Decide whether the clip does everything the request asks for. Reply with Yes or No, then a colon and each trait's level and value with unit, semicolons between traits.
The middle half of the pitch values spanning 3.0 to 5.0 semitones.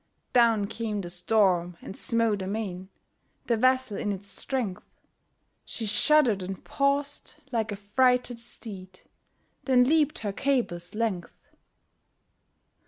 Yes: average, 4.4 semitones